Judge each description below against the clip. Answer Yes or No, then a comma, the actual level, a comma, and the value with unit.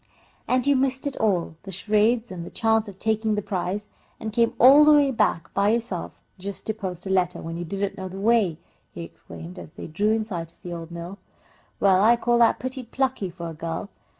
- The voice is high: Yes, high, 205 Hz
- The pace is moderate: No, fast, 230 wpm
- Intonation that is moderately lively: Yes, average, 4.6 semitones